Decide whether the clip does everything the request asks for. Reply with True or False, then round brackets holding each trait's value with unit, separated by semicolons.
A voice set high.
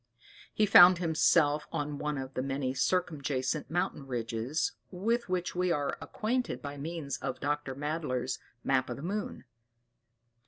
False (150 Hz)